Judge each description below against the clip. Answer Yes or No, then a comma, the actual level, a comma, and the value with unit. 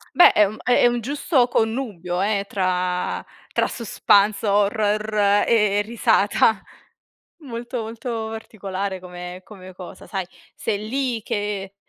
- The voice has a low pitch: No, high, 210 Hz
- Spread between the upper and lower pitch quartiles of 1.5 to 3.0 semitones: Yes, average, 2.7 semitones